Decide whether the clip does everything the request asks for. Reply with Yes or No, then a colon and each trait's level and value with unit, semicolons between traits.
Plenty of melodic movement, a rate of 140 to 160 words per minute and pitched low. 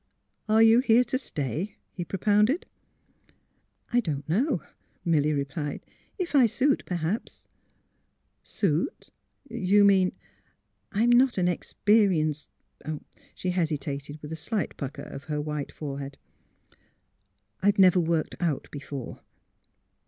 No: wide, 6.4 semitones; average, 155 wpm; medium, 175 Hz